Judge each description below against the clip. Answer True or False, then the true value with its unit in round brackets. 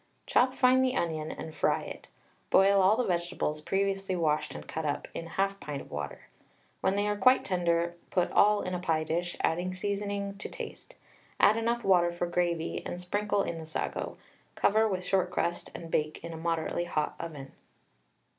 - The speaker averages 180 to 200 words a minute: True (185 wpm)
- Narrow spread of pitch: False (3.3 semitones)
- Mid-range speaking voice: True (180 Hz)